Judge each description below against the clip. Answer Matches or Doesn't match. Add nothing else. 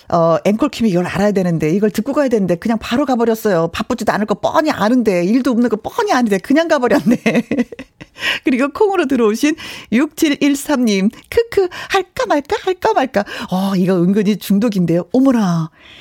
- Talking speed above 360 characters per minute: Doesn't match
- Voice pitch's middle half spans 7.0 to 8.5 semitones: Doesn't match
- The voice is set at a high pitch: Matches